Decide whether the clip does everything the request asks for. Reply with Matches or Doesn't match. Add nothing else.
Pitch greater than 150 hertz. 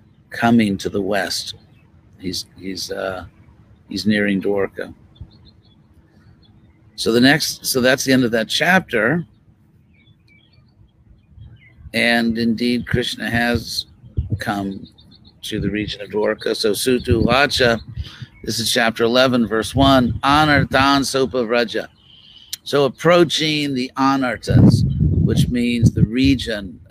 Doesn't match